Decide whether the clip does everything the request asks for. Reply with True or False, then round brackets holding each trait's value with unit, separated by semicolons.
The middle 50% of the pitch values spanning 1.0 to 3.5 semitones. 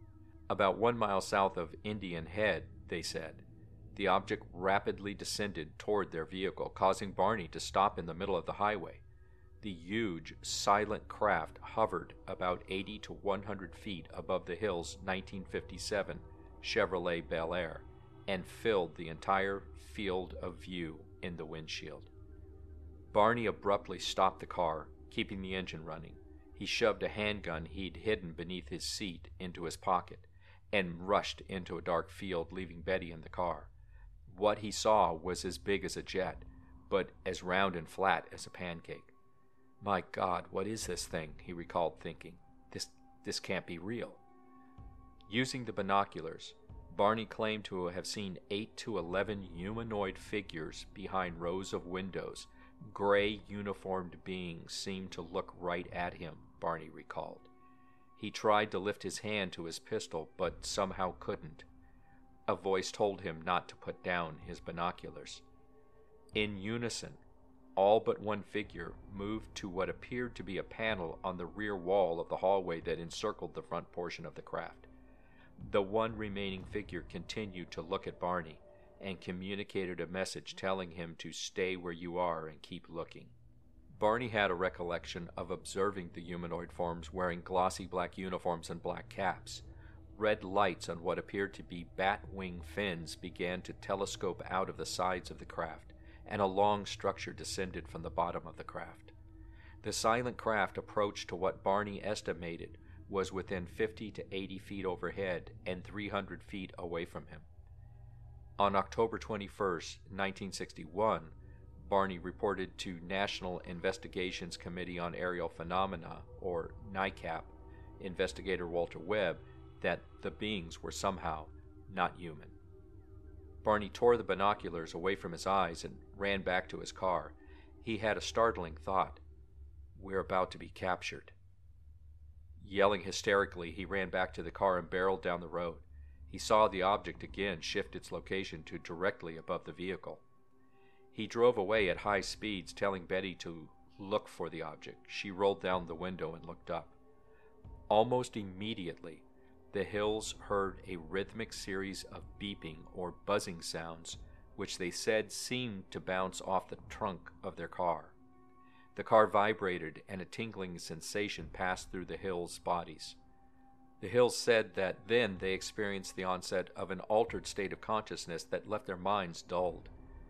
True (3.2 semitones)